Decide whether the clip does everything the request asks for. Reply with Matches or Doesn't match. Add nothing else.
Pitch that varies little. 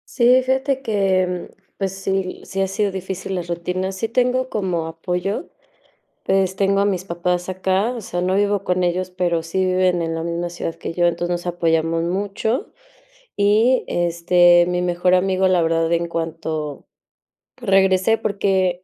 Matches